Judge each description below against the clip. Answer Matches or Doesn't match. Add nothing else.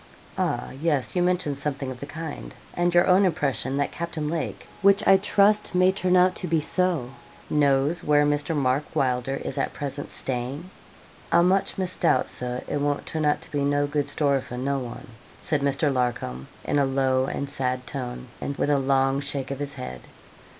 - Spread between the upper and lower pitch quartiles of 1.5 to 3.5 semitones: Doesn't match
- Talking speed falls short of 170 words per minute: Doesn't match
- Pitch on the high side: Doesn't match